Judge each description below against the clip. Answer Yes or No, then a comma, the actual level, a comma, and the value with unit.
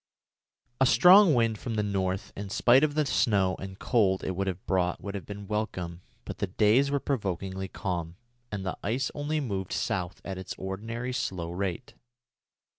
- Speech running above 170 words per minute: Yes, average, 180 wpm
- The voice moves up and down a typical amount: Yes, average, 4.2 semitones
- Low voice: Yes, low, 100 Hz